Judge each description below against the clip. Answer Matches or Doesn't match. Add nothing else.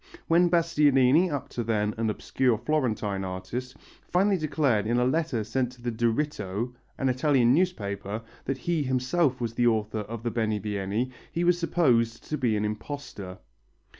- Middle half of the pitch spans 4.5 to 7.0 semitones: Matches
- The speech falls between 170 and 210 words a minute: Doesn't match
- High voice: Doesn't match